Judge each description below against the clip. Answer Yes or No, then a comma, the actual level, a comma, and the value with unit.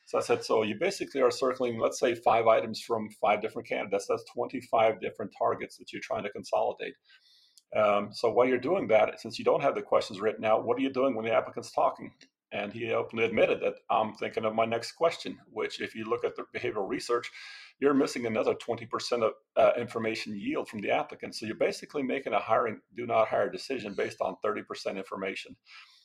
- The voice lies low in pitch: Yes, low, 120 Hz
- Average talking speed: No, fast, 210 wpm